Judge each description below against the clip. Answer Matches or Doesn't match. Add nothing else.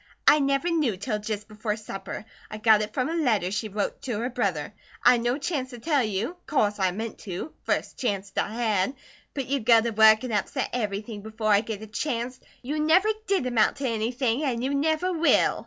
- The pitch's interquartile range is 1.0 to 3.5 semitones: Doesn't match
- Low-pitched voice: Doesn't match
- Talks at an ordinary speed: Doesn't match